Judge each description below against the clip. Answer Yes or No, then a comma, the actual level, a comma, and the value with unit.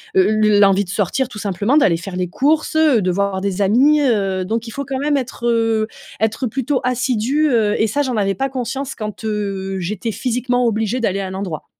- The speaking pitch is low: No, high, 220 Hz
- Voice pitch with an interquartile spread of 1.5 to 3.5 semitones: No, average, 4.7 semitones